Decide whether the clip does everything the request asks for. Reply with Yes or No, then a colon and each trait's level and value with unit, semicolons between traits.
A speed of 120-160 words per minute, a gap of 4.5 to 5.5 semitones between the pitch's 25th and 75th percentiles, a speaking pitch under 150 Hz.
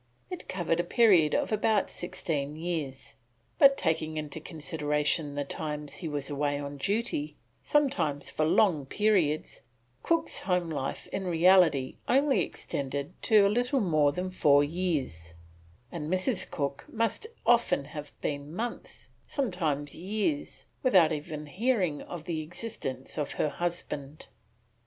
No: slow, 135 wpm; average, 4.9 semitones; medium, 160 Hz